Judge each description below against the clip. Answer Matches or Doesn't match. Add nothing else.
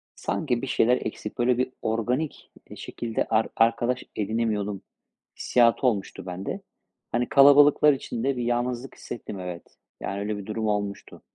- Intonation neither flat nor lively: Matches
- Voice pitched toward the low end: Matches